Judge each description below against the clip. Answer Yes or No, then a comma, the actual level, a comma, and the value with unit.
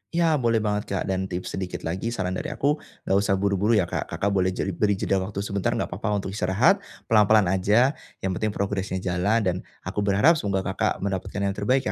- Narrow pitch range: Yes, narrow, 2.2 semitones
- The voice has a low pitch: Yes, low, 100 Hz